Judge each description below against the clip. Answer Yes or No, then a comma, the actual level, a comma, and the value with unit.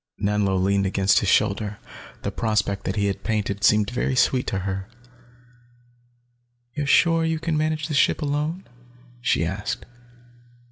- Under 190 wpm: Yes, average, 140 wpm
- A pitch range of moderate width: No, wide, 7.1 semitones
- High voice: No, low, 105 Hz